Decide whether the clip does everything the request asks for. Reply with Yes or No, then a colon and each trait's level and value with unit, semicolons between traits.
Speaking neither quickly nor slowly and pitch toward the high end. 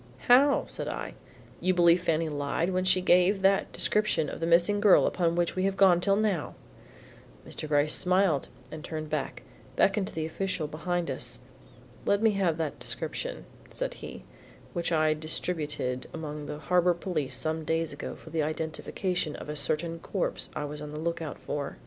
No: average, 180 wpm; medium, 165 Hz